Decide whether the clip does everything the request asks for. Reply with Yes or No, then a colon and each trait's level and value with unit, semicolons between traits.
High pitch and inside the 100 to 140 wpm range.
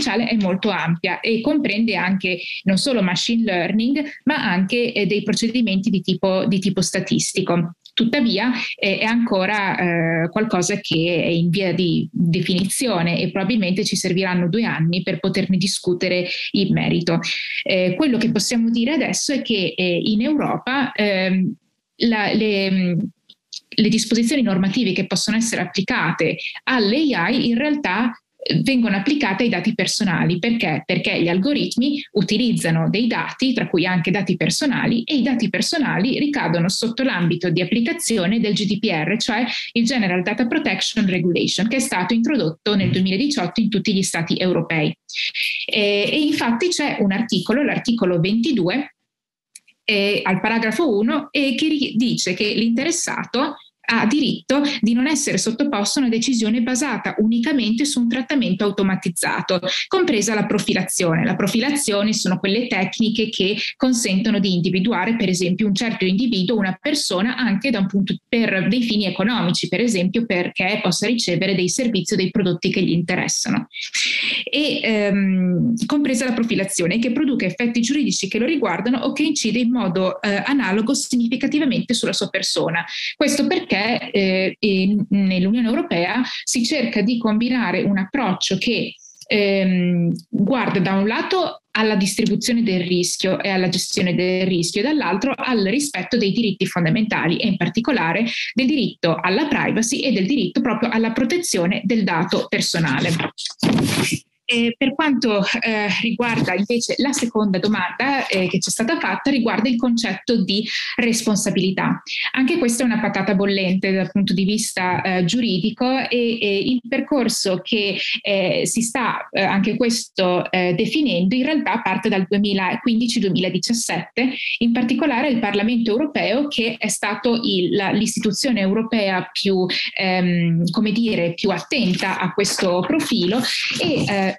No: high, 215 Hz; average, 150 wpm